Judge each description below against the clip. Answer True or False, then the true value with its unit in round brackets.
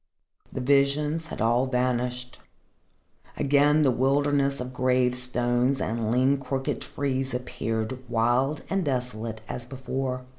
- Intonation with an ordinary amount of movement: False (2.0 semitones)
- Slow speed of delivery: True (115 wpm)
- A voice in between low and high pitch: False (130 Hz)